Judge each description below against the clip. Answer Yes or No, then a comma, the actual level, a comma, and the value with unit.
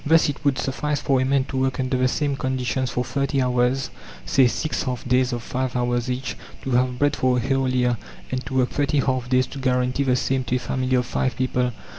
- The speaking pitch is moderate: No, low, 130 Hz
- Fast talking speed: Yes, fast, 235 wpm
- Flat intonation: Yes, narrow, 1.2 semitones